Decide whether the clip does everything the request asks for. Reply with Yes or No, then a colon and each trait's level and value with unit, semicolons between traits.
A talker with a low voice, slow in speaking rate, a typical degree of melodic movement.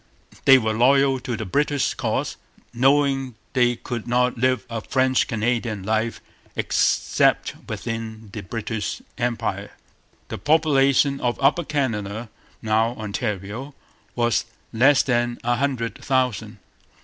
Yes: low, 120 Hz; slow, 120 wpm; average, 3.2 semitones